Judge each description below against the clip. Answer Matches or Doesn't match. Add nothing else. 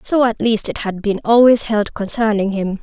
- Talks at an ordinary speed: Doesn't match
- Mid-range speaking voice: Doesn't match